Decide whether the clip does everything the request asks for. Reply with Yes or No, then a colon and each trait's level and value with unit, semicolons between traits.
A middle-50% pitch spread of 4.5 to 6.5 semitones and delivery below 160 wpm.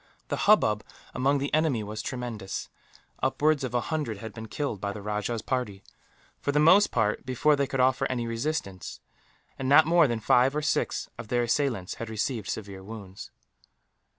No: average, 5.0 semitones; average, 180 wpm